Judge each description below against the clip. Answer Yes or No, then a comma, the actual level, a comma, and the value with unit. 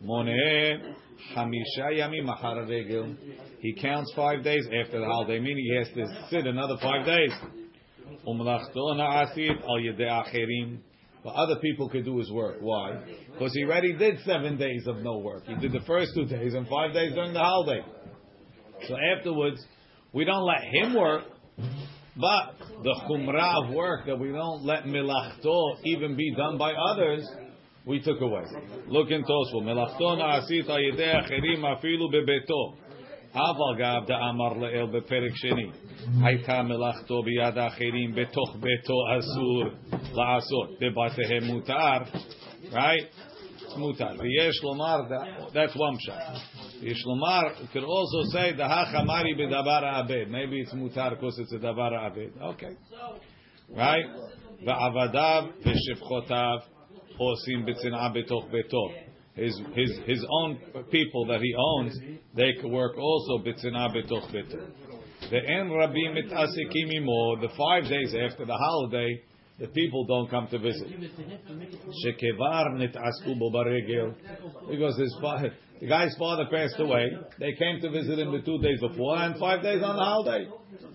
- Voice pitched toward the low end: Yes, low, 130 Hz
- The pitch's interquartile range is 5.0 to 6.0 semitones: No, average, 4.4 semitones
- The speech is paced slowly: Yes, slow, 125 wpm